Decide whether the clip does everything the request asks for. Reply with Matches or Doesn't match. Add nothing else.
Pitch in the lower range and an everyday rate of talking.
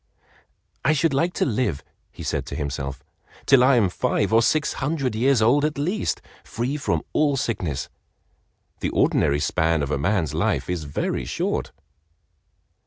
Matches